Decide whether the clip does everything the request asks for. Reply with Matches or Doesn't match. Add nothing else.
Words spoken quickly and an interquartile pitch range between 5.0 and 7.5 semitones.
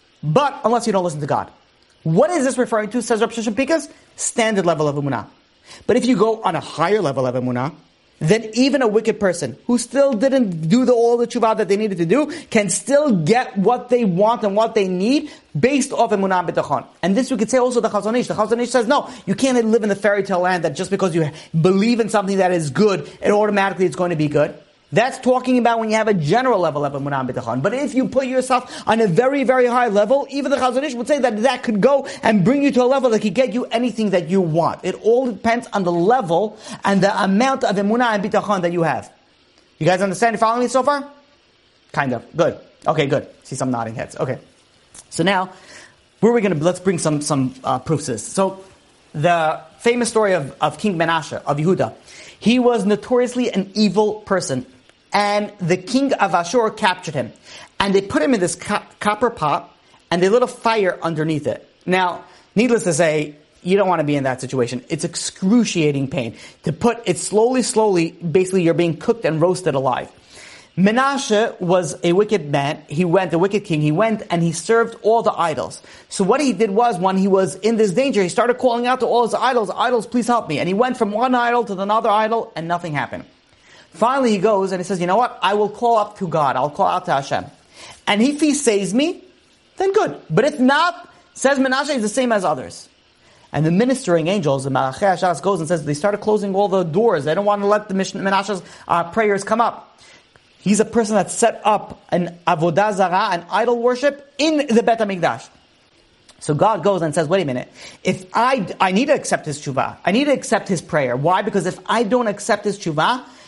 Matches